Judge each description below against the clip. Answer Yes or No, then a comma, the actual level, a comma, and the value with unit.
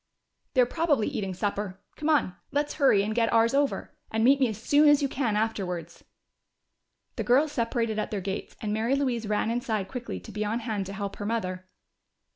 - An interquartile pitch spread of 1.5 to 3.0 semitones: No, average, 4.4 semitones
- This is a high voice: Yes, high, 225 Hz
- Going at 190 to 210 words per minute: Yes, average, 200 wpm